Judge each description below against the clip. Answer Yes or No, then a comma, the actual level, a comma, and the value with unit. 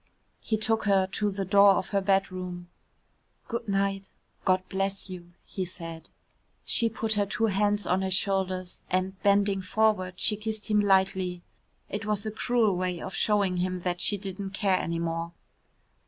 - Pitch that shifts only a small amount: Yes, narrow, 2.0 semitones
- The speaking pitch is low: No, high, 195 Hz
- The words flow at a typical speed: Yes, average, 170 wpm